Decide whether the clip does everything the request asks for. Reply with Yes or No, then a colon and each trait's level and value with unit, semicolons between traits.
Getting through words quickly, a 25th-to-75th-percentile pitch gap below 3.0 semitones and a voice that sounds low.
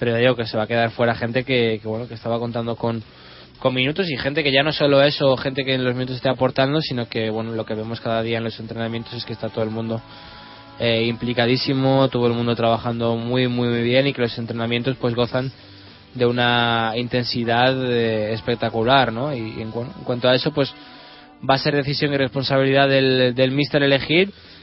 Yes: fast, 220 wpm; narrow, 2.6 semitones; low, 120 Hz